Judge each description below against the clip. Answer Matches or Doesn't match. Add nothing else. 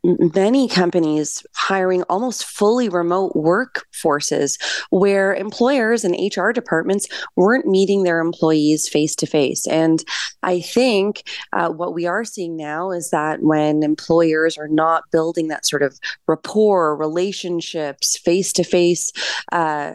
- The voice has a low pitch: Doesn't match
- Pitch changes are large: Doesn't match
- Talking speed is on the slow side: Matches